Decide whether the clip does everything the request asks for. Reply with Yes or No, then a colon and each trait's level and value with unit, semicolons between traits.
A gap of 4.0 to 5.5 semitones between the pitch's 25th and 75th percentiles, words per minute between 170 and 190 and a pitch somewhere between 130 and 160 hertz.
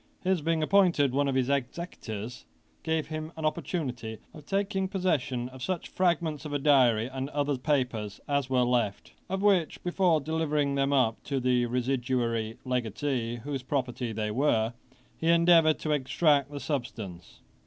No: average, 4.4 semitones; average, 155 wpm; medium, 140 Hz